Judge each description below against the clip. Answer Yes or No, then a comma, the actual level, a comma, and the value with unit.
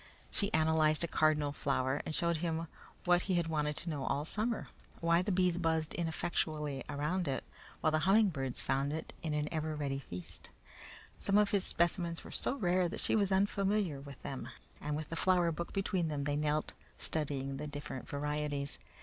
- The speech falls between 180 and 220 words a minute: Yes, average, 190 wpm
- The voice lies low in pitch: No, medium, 155 Hz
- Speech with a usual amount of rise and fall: Yes, average, 3.3 semitones